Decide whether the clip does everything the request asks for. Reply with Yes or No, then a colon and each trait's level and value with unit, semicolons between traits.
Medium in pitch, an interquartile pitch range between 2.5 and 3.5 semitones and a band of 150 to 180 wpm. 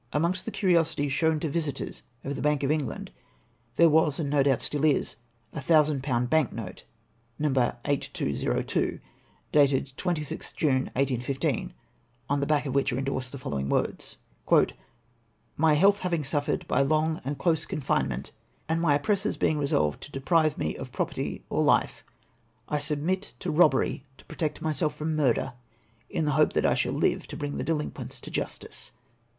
Yes: medium, 145 Hz; average, 2.8 semitones; average, 175 wpm